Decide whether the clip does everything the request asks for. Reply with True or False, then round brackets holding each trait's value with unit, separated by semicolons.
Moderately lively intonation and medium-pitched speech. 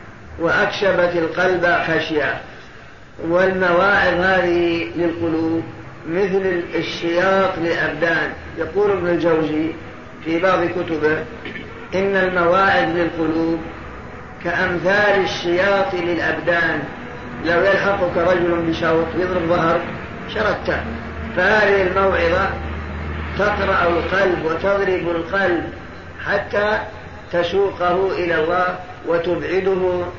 False (2.3 semitones; 175 Hz)